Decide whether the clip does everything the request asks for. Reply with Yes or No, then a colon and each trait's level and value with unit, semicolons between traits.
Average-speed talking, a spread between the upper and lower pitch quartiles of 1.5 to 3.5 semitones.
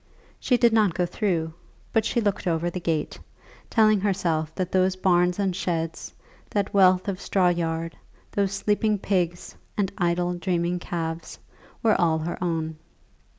Yes: average, 150 wpm; average, 2.8 semitones